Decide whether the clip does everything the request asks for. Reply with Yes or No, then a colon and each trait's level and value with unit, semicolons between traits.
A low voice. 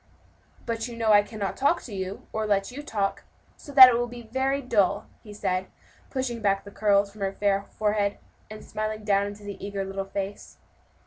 No: high, 210 Hz